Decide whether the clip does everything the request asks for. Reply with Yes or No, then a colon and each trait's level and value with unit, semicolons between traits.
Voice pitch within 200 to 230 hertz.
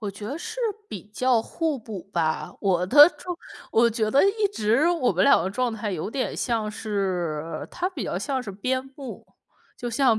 Yes: high, 225 Hz